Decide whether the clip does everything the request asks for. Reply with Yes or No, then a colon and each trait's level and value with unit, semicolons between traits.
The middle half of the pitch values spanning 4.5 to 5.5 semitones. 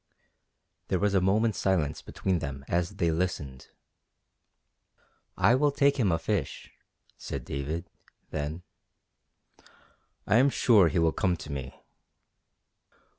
Yes: average, 5.2 semitones